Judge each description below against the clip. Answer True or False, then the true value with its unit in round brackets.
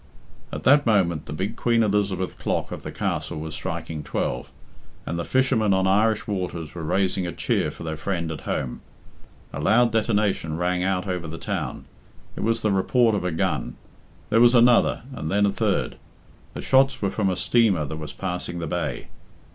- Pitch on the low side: True (95 Hz)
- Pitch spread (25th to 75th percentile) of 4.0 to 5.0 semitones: True (4.7 semitones)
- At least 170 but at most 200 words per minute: True (190 wpm)